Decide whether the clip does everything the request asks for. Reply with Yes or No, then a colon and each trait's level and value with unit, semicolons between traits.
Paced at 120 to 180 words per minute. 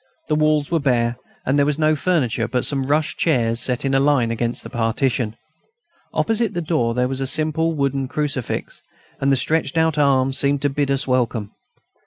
No: average, 195 wpm